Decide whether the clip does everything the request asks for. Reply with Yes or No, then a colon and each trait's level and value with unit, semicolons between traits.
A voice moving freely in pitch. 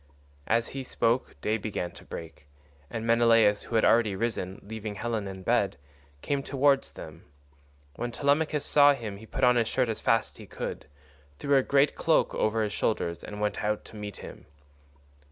No: average, 3.5 semitones